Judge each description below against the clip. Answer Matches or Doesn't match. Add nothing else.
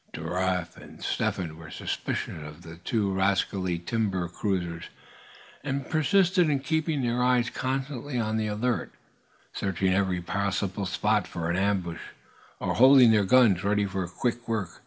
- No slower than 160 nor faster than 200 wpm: Doesn't match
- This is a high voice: Doesn't match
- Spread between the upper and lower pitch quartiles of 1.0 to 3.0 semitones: Doesn't match